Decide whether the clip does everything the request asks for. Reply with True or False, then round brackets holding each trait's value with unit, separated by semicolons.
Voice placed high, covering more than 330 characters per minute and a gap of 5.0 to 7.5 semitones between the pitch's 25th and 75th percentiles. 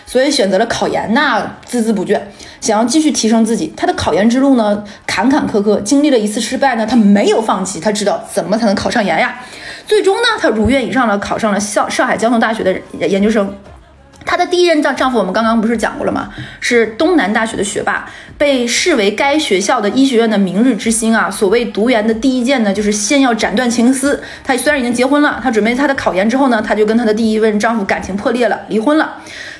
False (230 Hz; 350 characters per minute; 4.1 semitones)